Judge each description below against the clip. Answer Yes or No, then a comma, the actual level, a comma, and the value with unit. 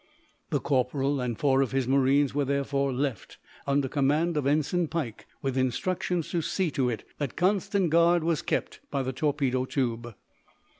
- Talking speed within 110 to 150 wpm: No, average, 165 wpm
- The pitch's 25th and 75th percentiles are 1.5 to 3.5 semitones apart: Yes, average, 3.1 semitones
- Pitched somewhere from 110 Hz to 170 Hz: Yes, medium, 140 Hz